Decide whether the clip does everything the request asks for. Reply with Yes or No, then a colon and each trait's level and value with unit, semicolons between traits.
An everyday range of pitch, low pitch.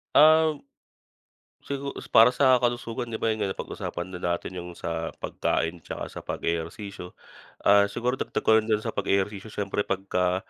Yes: average, 4.8 semitones; low, 100 Hz